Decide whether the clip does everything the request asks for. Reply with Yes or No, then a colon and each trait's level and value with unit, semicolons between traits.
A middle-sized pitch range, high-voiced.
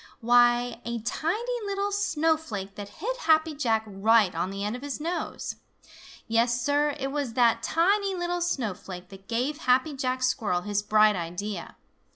No: wide, 7.0 semitones; high, 245 Hz